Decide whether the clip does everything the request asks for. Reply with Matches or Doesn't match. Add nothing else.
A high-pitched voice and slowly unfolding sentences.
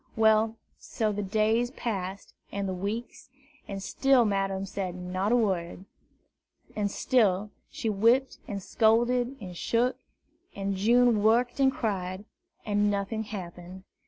Matches